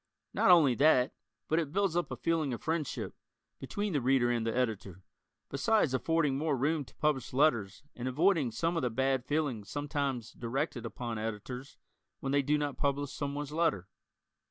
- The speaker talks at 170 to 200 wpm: Yes, average, 175 wpm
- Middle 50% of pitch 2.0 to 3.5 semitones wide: No, average, 4.2 semitones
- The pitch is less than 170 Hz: Yes, medium, 140 Hz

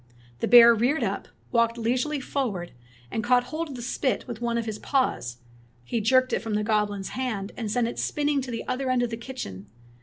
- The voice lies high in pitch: Yes, high, 235 Hz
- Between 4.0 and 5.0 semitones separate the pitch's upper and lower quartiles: No, average, 2.8 semitones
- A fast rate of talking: Yes, fast, 215 wpm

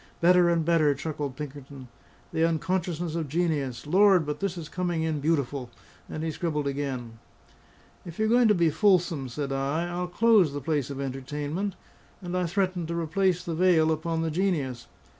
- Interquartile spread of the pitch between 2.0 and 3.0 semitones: No, average, 3.7 semitones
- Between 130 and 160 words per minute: No, average, 175 wpm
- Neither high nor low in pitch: Yes, medium, 160 Hz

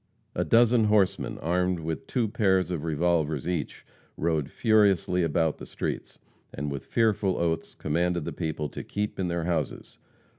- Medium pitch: No, very low, 85 Hz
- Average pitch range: Yes, average, 3.6 semitones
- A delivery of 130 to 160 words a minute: Yes, average, 155 wpm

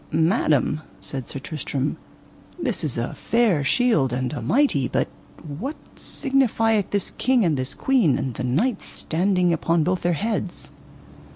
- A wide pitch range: Yes, wide, 8.8 semitones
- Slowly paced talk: No, average, 150 wpm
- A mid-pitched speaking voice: Yes, medium, 175 Hz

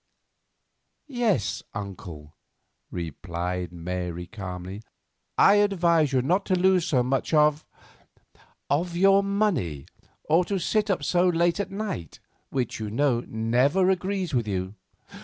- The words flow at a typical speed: No, slow, 125 wpm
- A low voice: No, medium, 145 Hz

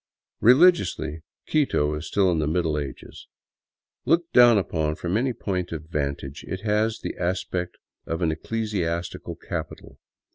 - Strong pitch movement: Yes, wide, 5.8 semitones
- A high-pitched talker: No, very low, 90 Hz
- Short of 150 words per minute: Yes, average, 140 wpm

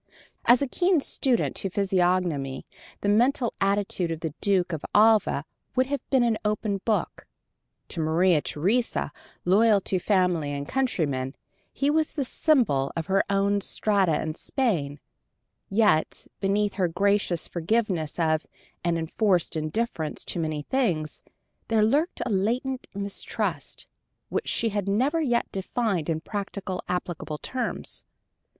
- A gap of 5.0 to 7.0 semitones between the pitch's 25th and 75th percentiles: Yes, wide, 5.6 semitones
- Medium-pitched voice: No, high, 195 Hz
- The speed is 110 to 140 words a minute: Yes, slow, 135 wpm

